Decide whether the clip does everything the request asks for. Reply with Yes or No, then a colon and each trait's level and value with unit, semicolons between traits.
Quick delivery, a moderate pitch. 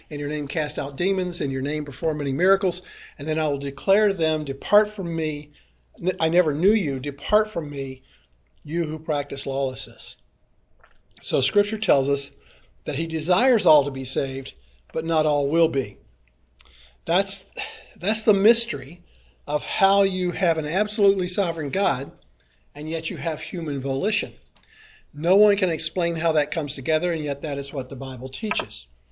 No: average, 170 wpm; medium, 155 Hz